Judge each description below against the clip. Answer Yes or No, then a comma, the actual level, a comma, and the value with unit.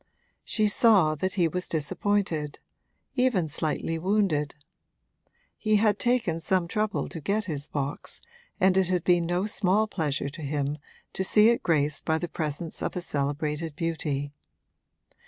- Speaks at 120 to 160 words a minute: Yes, average, 150 wpm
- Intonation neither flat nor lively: Yes, average, 5.0 semitones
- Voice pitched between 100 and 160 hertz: No, medium, 170 Hz